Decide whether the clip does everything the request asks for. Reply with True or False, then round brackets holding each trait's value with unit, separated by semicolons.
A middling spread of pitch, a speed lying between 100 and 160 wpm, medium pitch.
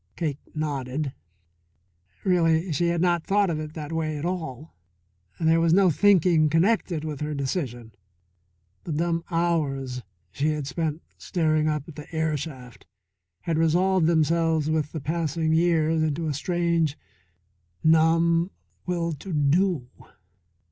False (2.1 semitones; 135 wpm; 160 Hz)